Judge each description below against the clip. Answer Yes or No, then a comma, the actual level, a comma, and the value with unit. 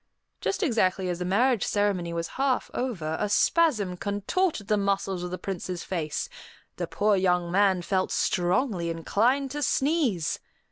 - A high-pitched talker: Yes, high, 195 Hz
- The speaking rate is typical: Yes, average, 150 wpm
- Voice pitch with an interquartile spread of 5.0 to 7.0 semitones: Yes, wide, 5.6 semitones